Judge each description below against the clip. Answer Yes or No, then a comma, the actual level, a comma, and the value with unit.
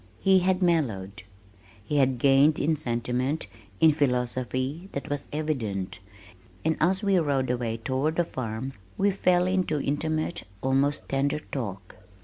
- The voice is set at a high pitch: No, medium, 140 Hz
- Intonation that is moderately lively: Yes, average, 4.3 semitones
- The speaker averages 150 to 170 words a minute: No, slow, 135 wpm